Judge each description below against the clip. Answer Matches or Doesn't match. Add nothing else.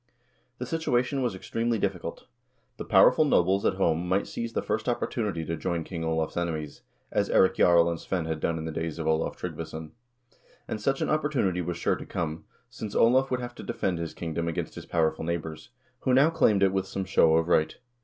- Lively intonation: Matches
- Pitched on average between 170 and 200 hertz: Doesn't match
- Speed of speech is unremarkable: Doesn't match